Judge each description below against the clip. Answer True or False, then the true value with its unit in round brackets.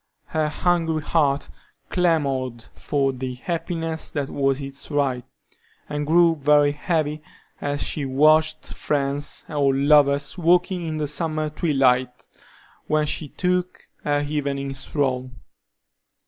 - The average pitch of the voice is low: False (145 Hz)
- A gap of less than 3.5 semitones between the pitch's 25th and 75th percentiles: True (2.4 semitones)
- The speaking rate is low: True (120 wpm)